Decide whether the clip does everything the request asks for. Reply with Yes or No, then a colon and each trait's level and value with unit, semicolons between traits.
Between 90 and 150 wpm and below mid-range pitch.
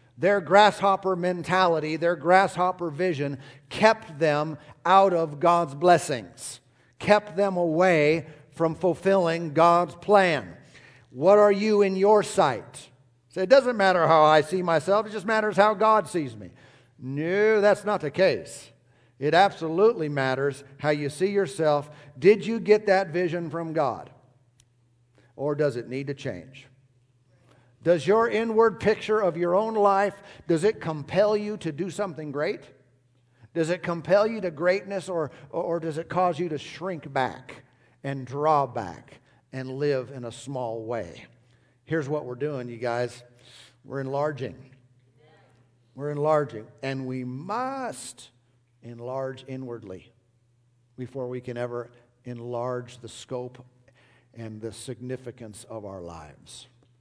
No: average, 140 wpm; medium, 145 Hz